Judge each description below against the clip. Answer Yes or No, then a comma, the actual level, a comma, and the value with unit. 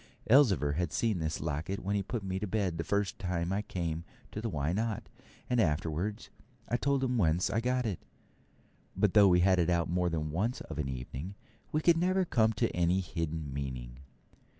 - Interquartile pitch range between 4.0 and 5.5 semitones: Yes, average, 5.2 semitones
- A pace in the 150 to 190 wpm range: No, average, 200 wpm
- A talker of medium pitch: No, very low, 90 Hz